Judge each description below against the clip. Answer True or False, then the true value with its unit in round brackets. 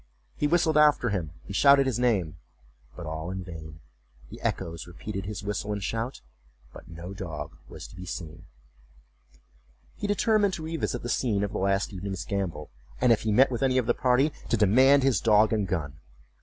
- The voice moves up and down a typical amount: False (7.0 semitones)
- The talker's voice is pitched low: True (100 Hz)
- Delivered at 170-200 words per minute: True (185 wpm)